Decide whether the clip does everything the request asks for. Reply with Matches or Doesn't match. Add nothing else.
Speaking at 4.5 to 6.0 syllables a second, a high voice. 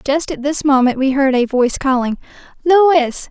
Matches